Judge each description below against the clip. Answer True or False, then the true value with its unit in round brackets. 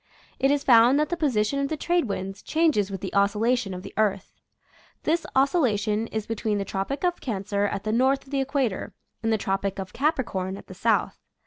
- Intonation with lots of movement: True (5.7 semitones)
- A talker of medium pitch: False (225 Hz)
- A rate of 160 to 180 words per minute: False (205 wpm)